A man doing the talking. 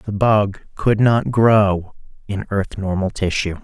Yes: male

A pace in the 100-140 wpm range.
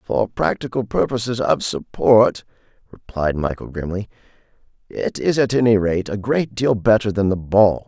No: average, 150 wpm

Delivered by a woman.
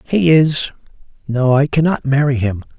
No: male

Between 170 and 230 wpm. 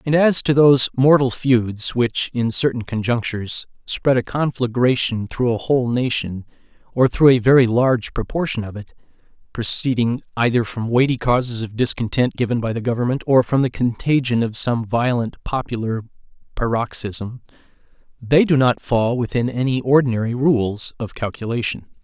No: average, 150 wpm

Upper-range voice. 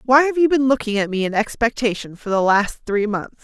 Yes: high, 230 Hz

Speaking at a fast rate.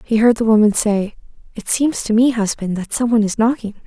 Yes: fast, 235 wpm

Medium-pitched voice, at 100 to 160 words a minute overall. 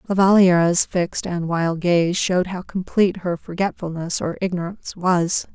Yes: medium, 180 Hz; average, 150 wpm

